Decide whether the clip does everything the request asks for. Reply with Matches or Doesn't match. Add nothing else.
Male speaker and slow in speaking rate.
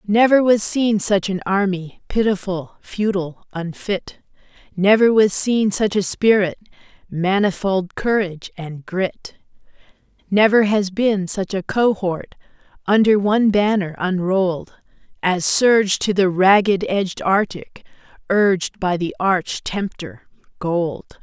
Doesn't match